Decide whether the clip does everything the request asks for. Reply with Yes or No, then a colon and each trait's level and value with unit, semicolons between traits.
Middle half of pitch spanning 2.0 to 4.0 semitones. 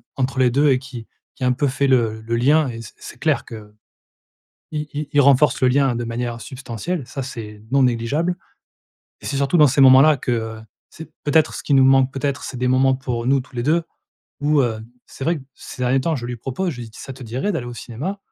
Yes: average, 3.0 semitones